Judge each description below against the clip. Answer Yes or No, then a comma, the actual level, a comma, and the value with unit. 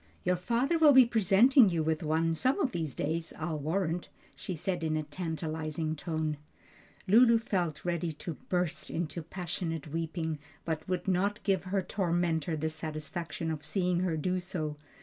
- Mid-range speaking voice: Yes, medium, 170 Hz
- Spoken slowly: No, average, 165 wpm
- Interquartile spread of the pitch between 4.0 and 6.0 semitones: No, average, 2.9 semitones